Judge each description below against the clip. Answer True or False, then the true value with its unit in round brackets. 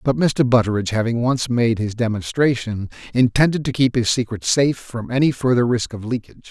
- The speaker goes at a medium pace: True (185 wpm)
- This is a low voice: True (120 Hz)